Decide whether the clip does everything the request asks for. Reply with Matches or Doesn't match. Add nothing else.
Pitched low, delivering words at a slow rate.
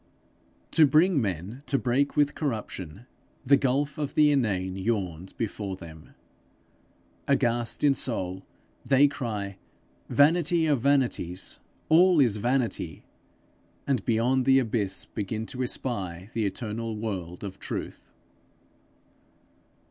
Matches